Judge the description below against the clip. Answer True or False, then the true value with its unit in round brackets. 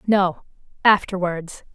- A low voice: False (185 Hz)